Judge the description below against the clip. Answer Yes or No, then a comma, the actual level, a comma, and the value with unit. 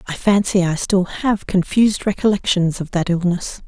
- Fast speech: No, average, 165 wpm